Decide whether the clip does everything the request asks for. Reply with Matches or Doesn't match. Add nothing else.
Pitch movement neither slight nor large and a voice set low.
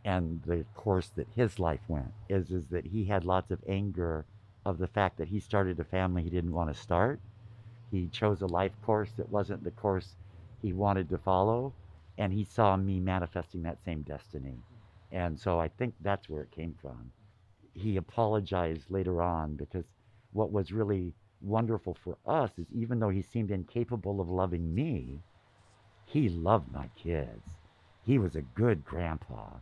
Matches